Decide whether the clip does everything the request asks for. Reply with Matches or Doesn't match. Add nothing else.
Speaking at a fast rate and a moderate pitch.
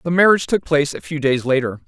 Matches